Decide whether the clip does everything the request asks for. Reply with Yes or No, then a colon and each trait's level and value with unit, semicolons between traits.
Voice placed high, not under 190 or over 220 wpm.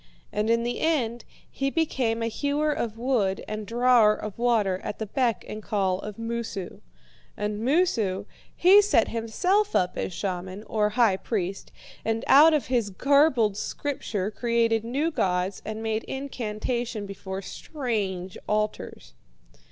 No: high, 225 Hz; average, 145 wpm